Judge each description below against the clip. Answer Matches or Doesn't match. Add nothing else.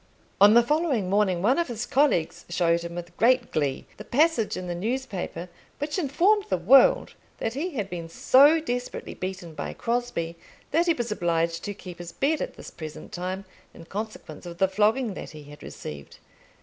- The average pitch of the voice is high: Matches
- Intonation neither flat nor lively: Doesn't match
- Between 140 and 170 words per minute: Doesn't match